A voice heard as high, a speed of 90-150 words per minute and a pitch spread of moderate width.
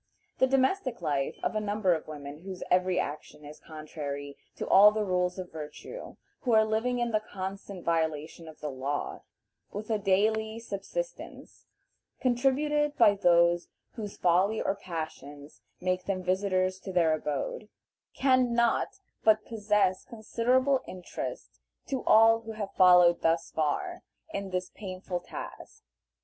Yes: high, 195 Hz; average, 145 wpm; average, 4.6 semitones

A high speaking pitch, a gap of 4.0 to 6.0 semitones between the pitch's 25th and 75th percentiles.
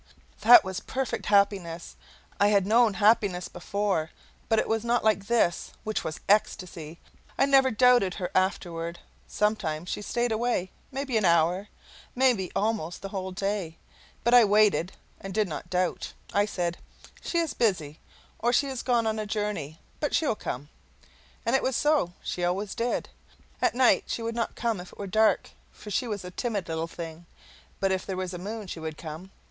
Yes: high, 200 Hz; average, 4.3 semitones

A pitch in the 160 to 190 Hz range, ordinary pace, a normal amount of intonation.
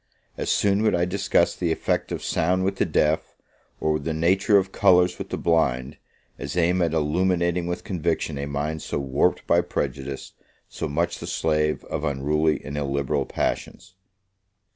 No: very low, 80 Hz; average, 165 wpm; average, 3.4 semitones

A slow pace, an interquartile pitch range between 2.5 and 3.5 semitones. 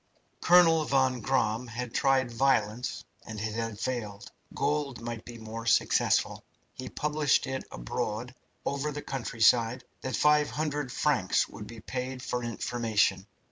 Yes: slow, 130 wpm; average, 3.1 semitones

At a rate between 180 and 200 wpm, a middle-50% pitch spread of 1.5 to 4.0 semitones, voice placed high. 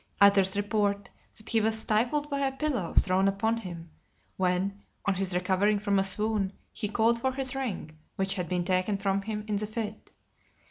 Yes: average, 185 wpm; narrow, 2.5 semitones; high, 200 Hz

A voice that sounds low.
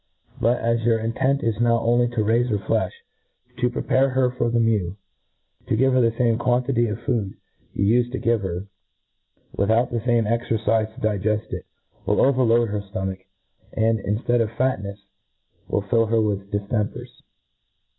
Yes: low, 115 Hz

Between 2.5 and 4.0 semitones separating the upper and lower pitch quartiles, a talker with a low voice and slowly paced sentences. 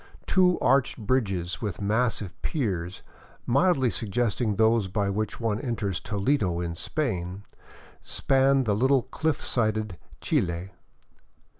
No: average, 5.2 semitones; low, 110 Hz; slow, 115 wpm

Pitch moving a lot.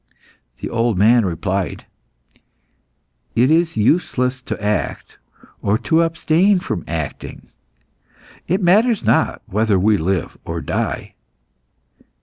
Yes: wide, 8.9 semitones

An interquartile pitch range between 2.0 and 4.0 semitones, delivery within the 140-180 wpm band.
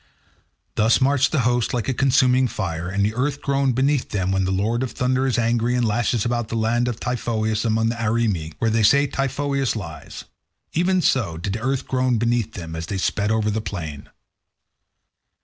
No: average, 3.6 semitones; average, 190 wpm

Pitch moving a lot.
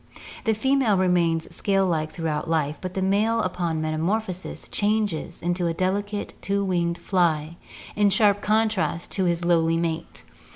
No: average, 3.5 semitones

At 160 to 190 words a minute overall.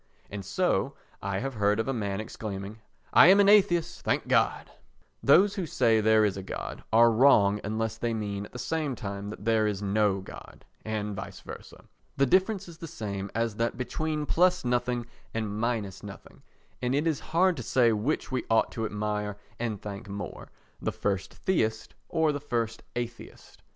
Yes: average, 180 wpm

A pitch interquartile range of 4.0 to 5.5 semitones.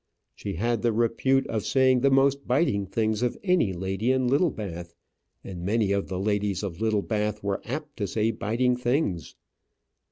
Yes: average, 4.5 semitones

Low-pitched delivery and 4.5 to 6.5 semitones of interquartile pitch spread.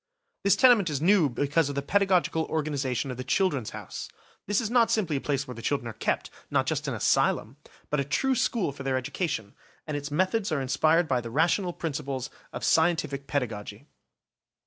No: medium, 150 Hz; average, 5.0 semitones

